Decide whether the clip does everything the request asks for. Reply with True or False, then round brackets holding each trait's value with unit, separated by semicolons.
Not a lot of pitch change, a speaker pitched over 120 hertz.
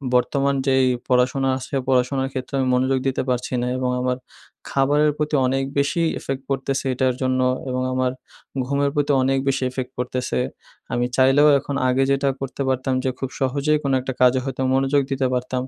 True (1.3 semitones; 135 Hz)